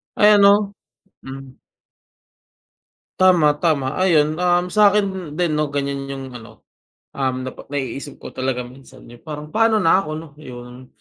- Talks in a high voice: No, medium, 150 Hz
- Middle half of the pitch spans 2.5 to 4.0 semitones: No, wide, 5.6 semitones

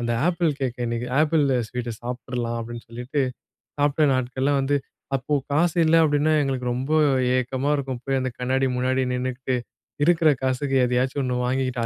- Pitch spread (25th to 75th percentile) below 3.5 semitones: Yes, narrow, 2.5 semitones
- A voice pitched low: Yes, low, 130 Hz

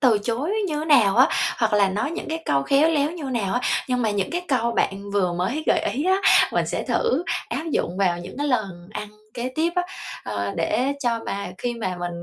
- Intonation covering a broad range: Yes, wide, 6.9 semitones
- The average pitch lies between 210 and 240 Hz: Yes, high, 235 Hz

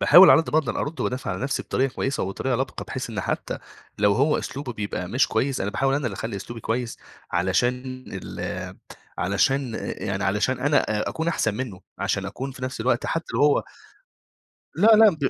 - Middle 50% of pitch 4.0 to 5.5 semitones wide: Yes, average, 4.8 semitones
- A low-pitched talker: Yes, low, 125 Hz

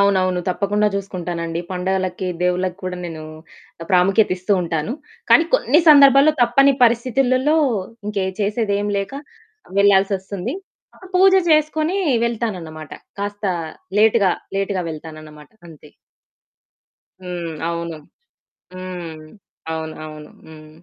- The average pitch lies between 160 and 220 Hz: Yes, high, 190 Hz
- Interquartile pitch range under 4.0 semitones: No, average, 4.9 semitones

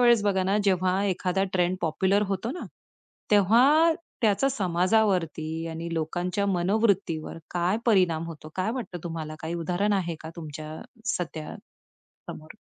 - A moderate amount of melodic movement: Yes, average, 3.6 semitones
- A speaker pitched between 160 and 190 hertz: Yes, medium, 185 Hz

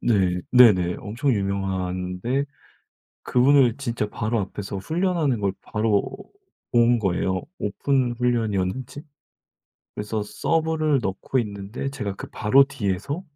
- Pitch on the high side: No, low, 110 Hz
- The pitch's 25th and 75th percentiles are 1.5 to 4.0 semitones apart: No, wide, 5.4 semitones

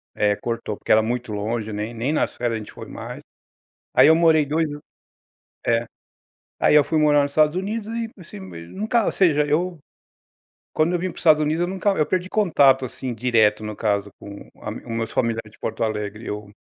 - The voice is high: No, low, 135 Hz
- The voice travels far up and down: Yes, wide, 7.0 semitones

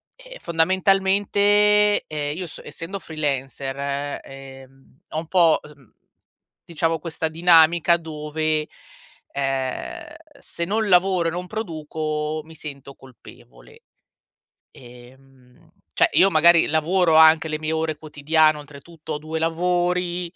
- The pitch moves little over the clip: No, average, 3.2 semitones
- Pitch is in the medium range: Yes, medium, 160 Hz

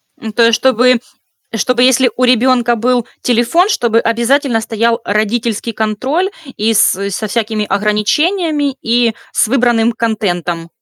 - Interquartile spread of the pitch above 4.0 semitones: No, average, 2.7 semitones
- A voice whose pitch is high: Yes, high, 235 Hz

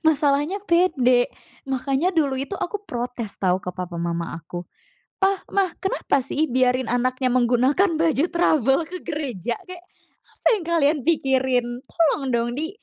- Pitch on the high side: Yes, very high, 270 Hz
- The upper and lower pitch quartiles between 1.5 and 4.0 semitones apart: No, average, 5.2 semitones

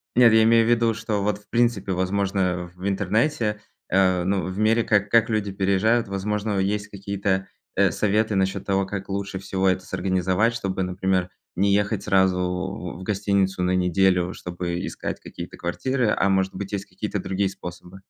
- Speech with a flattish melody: Yes, narrow, 2.0 semitones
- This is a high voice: No, very low, 95 Hz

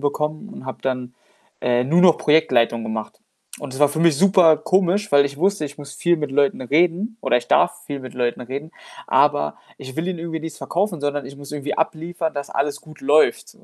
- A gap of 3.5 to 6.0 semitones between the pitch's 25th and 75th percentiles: Yes, average, 3.9 semitones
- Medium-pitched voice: Yes, medium, 145 Hz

